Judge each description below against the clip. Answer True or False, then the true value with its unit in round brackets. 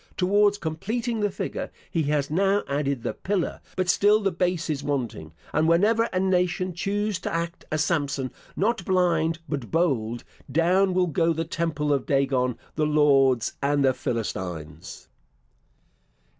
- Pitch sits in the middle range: True (165 Hz)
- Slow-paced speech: False (150 wpm)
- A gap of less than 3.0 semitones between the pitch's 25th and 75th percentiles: False (5.1 semitones)